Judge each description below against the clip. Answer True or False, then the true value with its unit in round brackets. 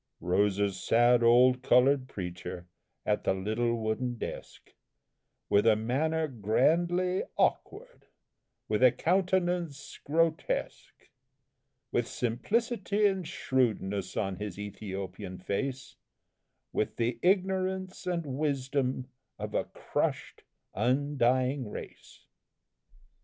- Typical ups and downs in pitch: False (7.5 semitones)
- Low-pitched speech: True (130 Hz)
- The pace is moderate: False (100 wpm)